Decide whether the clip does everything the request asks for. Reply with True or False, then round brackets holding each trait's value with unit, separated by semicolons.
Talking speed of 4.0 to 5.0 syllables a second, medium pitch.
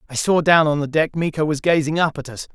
False (6.0 syllables/s; 155 Hz)